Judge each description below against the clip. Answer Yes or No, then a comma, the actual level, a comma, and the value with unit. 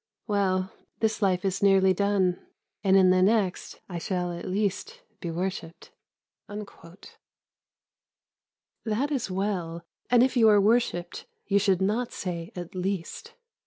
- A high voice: Yes, high, 195 Hz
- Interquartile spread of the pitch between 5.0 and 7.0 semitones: No, narrow, 2.5 semitones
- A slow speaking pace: Yes, slow, 130 wpm